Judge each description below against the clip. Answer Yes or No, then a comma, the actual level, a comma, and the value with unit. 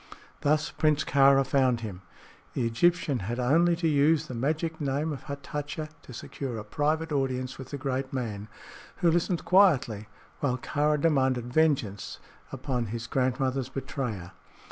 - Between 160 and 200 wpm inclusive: No, average, 145 wpm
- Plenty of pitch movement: No, average, 3.5 semitones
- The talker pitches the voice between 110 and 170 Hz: Yes, low, 135 Hz